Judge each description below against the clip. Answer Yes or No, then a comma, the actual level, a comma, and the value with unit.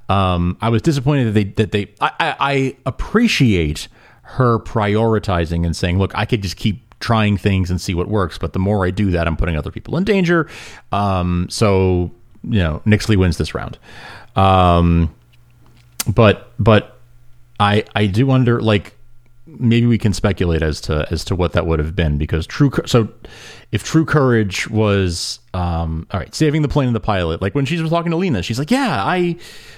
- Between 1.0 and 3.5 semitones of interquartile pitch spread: No, average, 5.2 semitones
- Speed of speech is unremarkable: Yes, average, 190 wpm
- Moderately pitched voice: No, low, 105 Hz